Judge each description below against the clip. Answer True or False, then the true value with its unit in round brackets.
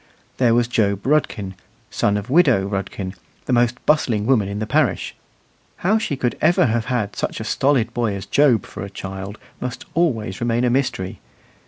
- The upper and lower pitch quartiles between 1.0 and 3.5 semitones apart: False (4.6 semitones)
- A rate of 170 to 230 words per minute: True (180 wpm)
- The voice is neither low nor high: False (120 Hz)